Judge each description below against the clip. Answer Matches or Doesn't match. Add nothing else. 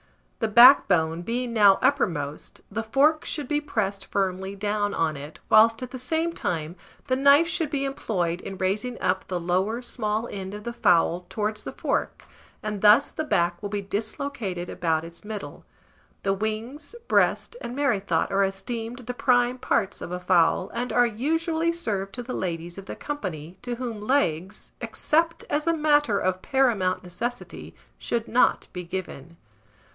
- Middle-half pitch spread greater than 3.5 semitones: Matches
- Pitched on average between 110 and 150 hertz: Doesn't match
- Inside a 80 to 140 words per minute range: Doesn't match